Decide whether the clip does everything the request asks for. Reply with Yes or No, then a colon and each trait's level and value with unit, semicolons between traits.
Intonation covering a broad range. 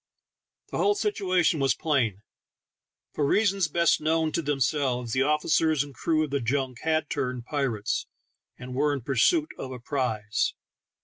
No: average, 3.9 semitones